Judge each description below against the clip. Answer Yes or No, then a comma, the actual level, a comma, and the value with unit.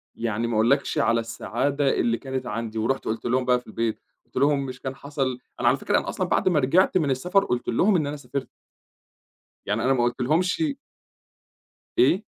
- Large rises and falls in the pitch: No, average, 3.8 semitones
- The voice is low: Yes, low, 130 Hz